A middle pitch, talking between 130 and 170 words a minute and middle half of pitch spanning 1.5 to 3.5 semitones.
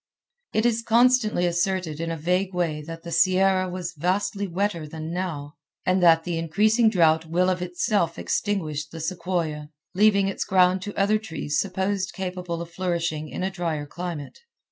Yes: medium, 180 Hz; average, 165 wpm; average, 2.7 semitones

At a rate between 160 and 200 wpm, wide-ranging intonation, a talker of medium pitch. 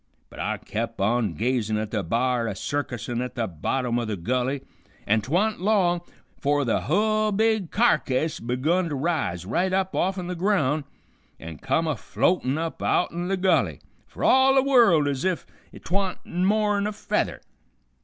Yes: average, 175 wpm; wide, 7.7 semitones; medium, 155 Hz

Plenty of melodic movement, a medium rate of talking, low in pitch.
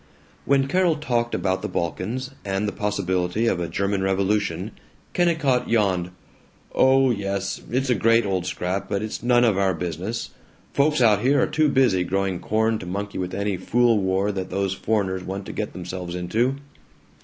No: average, 4.3 semitones; average, 175 wpm; low, 100 Hz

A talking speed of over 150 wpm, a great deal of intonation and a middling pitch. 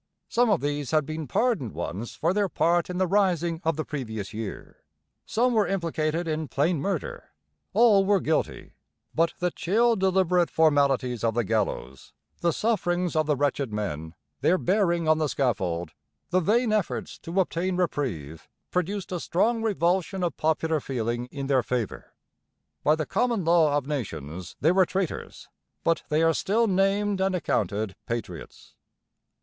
Yes: average, 160 wpm; wide, 6.2 semitones; medium, 165 Hz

